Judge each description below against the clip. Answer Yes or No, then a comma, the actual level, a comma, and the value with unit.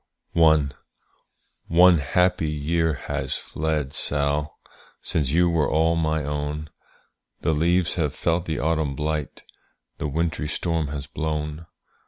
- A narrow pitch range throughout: Yes, narrow, 1.9 semitones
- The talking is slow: Yes, slow, 120 wpm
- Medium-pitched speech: No, very low, 75 Hz